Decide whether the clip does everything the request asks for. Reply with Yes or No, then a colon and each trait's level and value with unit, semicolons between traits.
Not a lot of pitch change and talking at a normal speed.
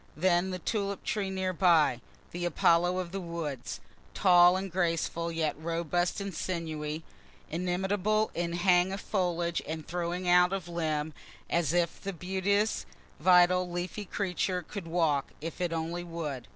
Yes: narrow, 1.9 semitones; average, 150 wpm